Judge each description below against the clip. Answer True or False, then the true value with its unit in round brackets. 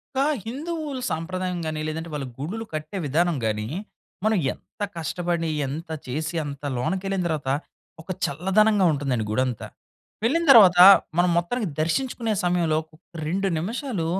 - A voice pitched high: False (175 Hz)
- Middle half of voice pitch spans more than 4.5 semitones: True (5.4 semitones)